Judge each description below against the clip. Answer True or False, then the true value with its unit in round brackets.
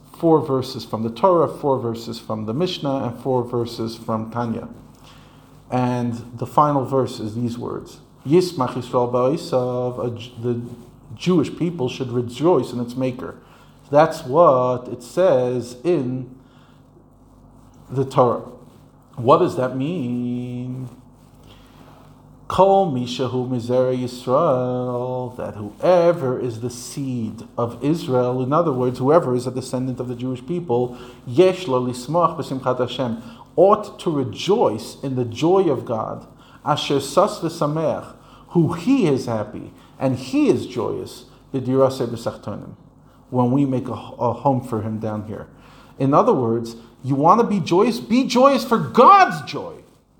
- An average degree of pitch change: False (2.1 semitones)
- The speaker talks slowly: True (120 wpm)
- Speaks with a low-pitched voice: True (125 Hz)